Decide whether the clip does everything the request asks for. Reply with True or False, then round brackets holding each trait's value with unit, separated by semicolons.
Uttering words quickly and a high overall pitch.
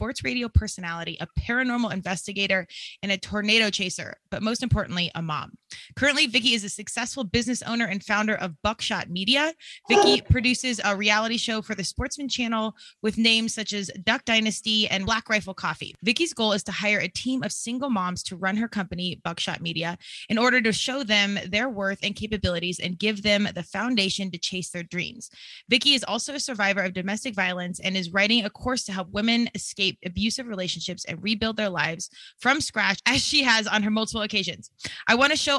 False (195 wpm; 210 Hz)